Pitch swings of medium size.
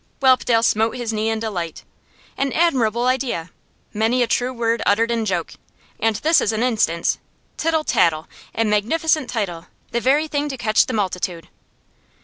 Yes: average, 3.5 semitones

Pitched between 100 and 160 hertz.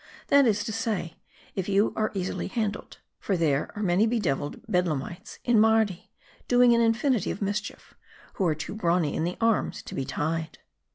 No: high, 200 Hz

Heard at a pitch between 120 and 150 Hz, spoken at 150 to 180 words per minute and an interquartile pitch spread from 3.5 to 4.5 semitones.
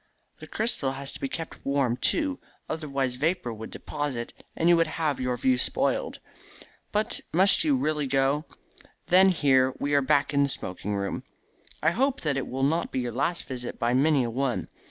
No: medium, 140 Hz; average, 190 wpm; average, 4.1 semitones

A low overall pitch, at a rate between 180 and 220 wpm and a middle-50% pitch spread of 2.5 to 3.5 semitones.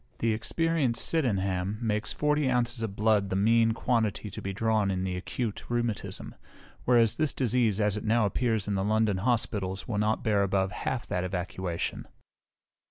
No: low, 110 Hz; average, 165 wpm; average, 3.2 semitones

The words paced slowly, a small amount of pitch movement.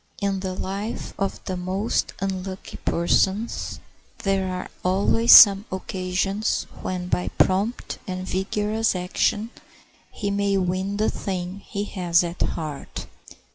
Yes: slow, 125 wpm; narrow, 1.7 semitones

